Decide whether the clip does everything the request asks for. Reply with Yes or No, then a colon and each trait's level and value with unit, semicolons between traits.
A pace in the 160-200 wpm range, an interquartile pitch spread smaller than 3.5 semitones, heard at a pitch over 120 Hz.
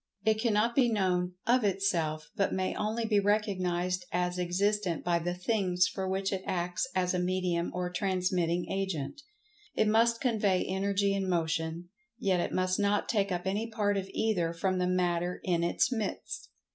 Yes: average, 170 wpm; narrow, 2.6 semitones; medium, 185 Hz